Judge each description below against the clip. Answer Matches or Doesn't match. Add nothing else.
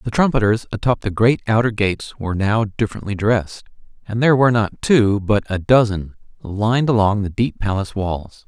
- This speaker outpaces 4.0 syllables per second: Matches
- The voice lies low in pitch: Matches